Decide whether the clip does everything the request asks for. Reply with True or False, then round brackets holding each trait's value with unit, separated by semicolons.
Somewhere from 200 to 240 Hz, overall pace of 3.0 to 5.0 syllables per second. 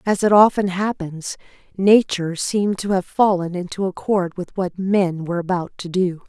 False (185 Hz; 4.8 syllables/s)